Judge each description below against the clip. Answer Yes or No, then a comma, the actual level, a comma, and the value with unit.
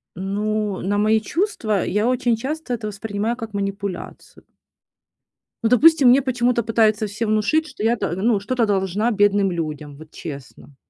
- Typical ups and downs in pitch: Yes, average, 3.3 semitones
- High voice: Yes, high, 215 Hz